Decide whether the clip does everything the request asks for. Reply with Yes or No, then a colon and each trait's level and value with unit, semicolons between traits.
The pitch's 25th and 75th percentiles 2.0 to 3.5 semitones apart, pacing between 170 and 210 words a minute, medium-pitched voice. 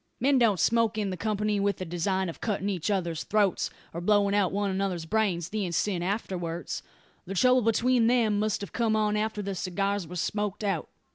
No: average, 2.7 semitones; average, 195 wpm; high, 200 Hz